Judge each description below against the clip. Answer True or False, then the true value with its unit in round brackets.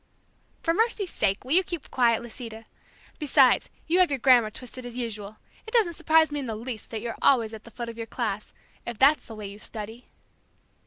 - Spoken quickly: True (210 wpm)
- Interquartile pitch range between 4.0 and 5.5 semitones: True (4.7 semitones)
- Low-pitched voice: False (240 Hz)